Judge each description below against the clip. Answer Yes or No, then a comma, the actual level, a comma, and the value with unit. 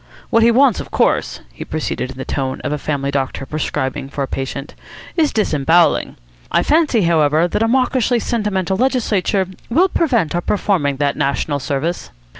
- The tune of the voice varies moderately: No, wide, 8.3 semitones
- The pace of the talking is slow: No, average, 170 wpm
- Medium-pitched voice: Yes, medium, 170 Hz